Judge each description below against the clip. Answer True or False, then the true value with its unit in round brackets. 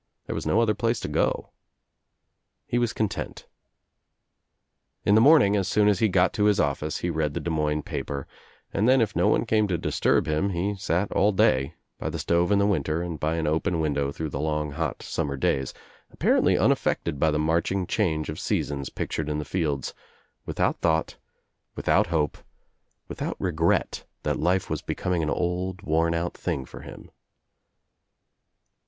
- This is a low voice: True (85 Hz)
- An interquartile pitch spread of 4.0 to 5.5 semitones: True (4.6 semitones)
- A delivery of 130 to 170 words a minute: False (180 wpm)